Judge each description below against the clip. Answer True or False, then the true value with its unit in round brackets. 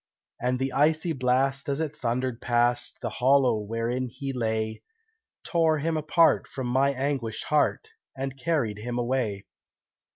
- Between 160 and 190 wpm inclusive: False (140 wpm)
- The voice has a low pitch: True (130 Hz)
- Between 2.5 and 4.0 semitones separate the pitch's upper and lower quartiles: True (2.9 semitones)